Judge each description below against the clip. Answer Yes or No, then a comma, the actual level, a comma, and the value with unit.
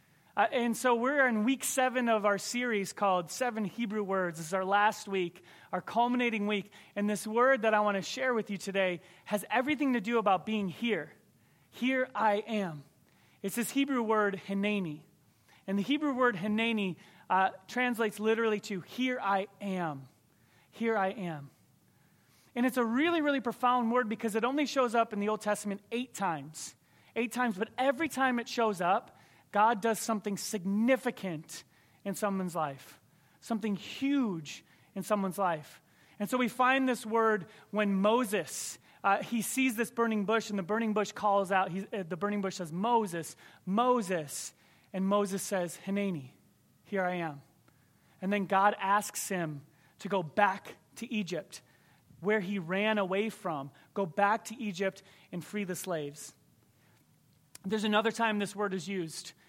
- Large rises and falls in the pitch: No, average, 4.0 semitones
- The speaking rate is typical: Yes, average, 165 wpm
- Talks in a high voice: Yes, high, 205 Hz